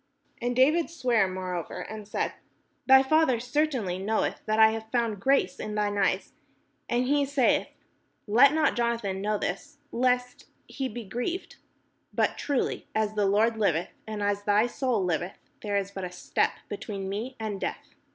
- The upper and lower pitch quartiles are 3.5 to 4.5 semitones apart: Yes, average, 4.2 semitones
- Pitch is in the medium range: No, high, 220 Hz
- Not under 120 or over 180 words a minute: Yes, average, 175 wpm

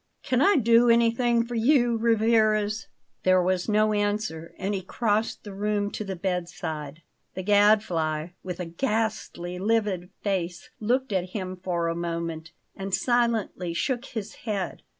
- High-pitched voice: Yes, high, 205 Hz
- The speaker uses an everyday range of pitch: Yes, average, 4.1 semitones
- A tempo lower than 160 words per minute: Yes, average, 150 wpm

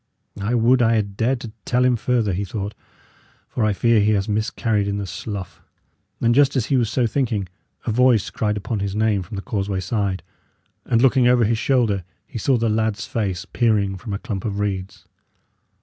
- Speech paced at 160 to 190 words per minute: No, average, 200 wpm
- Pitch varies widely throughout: No, average, 2.9 semitones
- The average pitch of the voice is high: No, low, 110 Hz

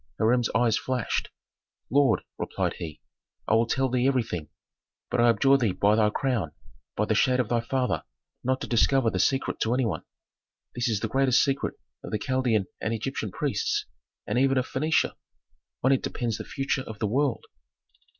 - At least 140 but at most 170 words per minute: No, average, 180 wpm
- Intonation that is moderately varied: Yes, average, 3.2 semitones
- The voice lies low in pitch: Yes, low, 120 Hz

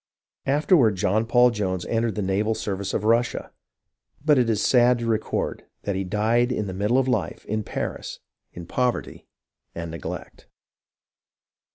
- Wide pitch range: No, average, 3.7 semitones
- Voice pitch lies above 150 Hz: No, low, 110 Hz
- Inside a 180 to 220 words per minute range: No, average, 145 wpm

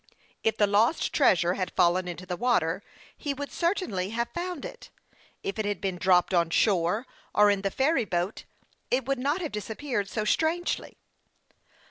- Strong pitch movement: Yes, wide, 6.7 semitones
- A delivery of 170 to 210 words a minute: Yes, average, 175 wpm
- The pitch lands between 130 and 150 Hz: No, high, 210 Hz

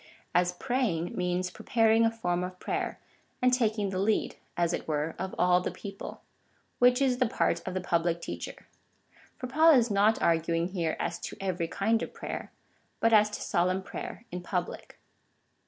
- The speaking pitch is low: No, high, 190 Hz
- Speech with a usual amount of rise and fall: Yes, average, 4.3 semitones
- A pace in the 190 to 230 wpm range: No, average, 180 wpm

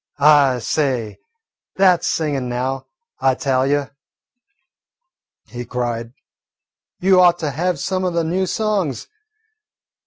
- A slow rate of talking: Yes, slow, 120 wpm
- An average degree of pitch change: No, wide, 5.7 semitones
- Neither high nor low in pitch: Yes, medium, 145 Hz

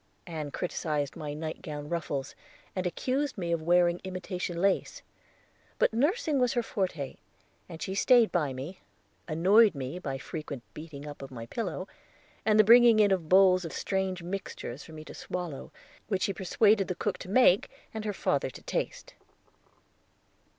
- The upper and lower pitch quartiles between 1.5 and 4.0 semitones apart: No, average, 4.8 semitones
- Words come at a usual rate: Yes, average, 165 wpm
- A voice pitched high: No, medium, 180 Hz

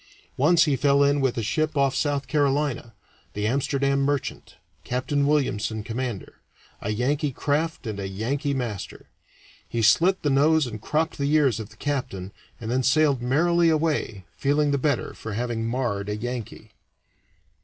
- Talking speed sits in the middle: Yes, average, 160 wpm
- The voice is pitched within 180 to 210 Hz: No, low, 135 Hz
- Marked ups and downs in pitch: No, average, 4.2 semitones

